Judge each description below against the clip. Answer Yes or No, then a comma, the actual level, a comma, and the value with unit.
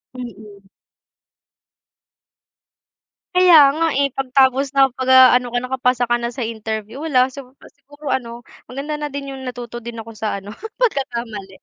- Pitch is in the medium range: No, very high, 250 Hz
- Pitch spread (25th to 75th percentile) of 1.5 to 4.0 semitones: Yes, average, 2.9 semitones